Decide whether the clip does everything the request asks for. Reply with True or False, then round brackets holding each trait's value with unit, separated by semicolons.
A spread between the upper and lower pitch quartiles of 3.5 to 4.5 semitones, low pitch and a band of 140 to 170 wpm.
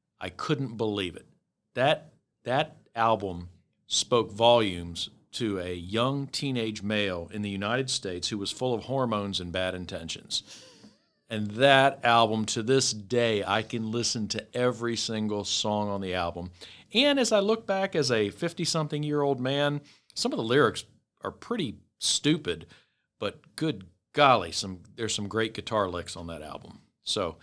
False (5.3 semitones; 110 Hz; 160 wpm)